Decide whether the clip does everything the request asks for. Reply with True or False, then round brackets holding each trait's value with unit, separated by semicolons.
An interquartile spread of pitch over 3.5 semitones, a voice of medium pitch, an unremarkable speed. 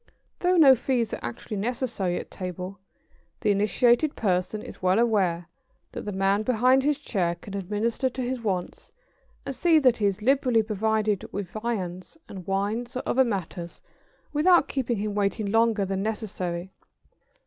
False (4.1 semitones; 215 Hz; 160 wpm)